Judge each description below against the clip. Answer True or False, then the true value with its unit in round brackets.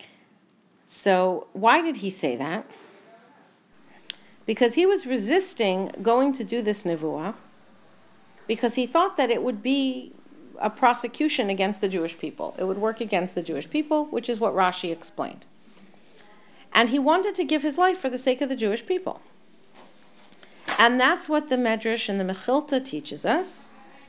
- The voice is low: False (240 Hz)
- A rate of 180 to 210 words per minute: False (160 wpm)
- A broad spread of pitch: True (7.2 semitones)